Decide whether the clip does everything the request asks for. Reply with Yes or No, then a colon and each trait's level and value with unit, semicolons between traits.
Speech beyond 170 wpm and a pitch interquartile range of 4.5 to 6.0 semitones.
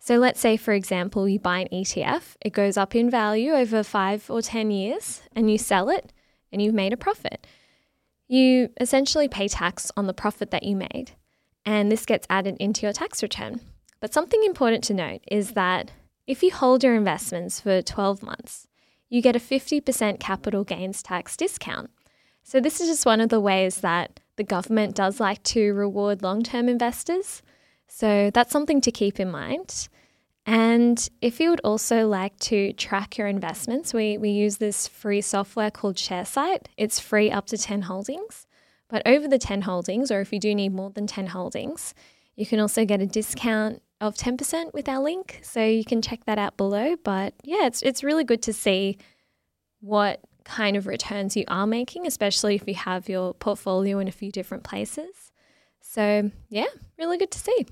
No: average, 190 wpm; average, 3.7 semitones